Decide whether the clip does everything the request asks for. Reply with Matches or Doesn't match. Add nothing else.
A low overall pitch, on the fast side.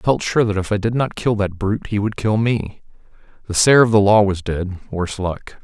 Matches